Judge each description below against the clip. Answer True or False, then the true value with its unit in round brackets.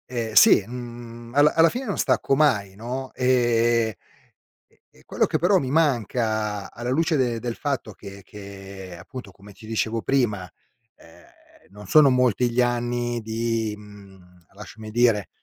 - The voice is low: True (115 Hz)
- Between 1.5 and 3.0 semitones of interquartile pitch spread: False (3.4 semitones)